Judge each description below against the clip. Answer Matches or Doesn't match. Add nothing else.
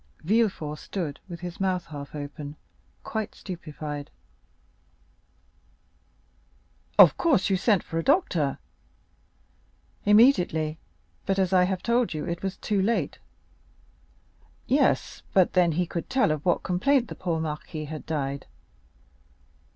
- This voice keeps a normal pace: Doesn't match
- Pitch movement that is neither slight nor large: Matches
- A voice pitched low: Doesn't match